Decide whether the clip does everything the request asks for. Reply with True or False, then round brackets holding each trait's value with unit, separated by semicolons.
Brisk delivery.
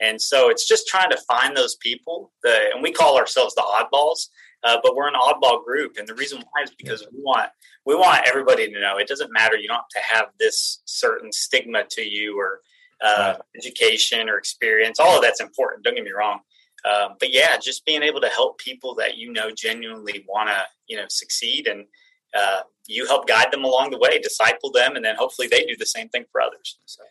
True (225 wpm)